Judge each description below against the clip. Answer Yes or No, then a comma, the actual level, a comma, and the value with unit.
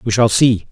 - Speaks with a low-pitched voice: Yes, low, 105 Hz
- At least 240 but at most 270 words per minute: Yes, fast, 250 wpm